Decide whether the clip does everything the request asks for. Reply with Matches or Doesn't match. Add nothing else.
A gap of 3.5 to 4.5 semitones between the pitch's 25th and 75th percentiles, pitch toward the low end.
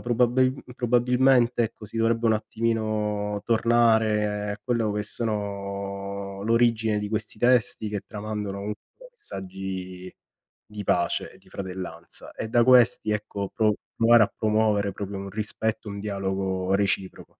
Doesn't match